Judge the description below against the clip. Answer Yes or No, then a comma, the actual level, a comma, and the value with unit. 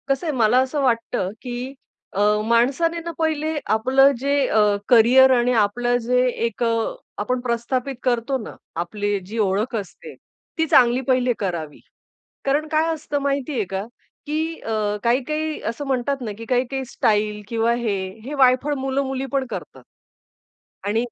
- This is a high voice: Yes, very high, 250 Hz